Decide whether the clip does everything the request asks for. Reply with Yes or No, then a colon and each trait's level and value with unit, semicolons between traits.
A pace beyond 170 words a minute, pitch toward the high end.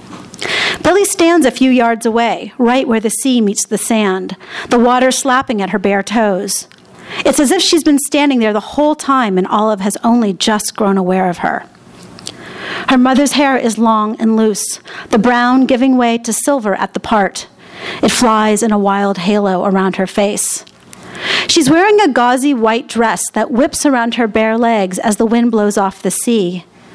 Yes: average, 185 wpm; high, 230 Hz